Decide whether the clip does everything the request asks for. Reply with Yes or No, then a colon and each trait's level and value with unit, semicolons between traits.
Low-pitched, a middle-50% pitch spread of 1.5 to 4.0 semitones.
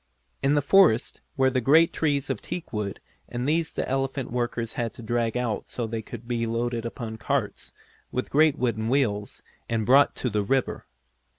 Yes: low, 120 Hz; average, 3.1 semitones